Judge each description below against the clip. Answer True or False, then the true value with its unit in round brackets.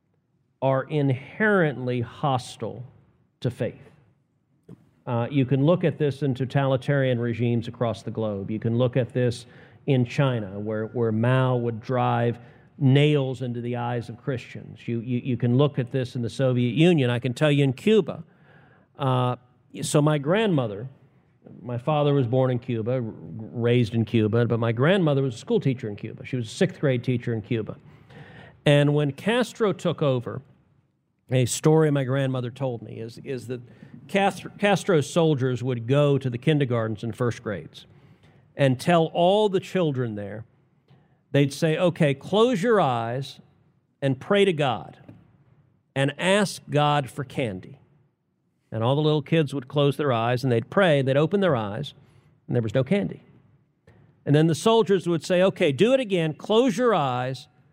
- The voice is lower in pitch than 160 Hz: True (135 Hz)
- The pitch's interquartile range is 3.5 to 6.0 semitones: True (3.8 semitones)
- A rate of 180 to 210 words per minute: False (170 wpm)